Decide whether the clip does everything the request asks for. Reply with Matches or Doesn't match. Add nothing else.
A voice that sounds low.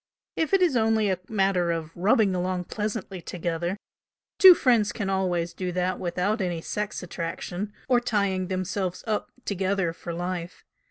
Doesn't match